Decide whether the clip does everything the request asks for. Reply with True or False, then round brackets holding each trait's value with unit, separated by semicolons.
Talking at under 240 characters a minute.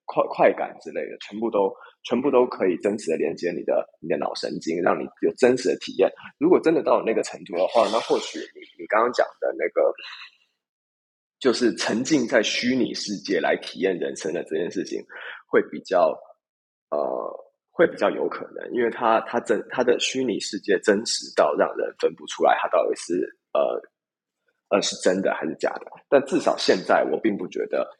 False (275 characters per minute)